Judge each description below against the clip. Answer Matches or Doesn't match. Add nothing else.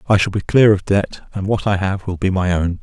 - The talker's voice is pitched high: Doesn't match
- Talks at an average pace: Doesn't match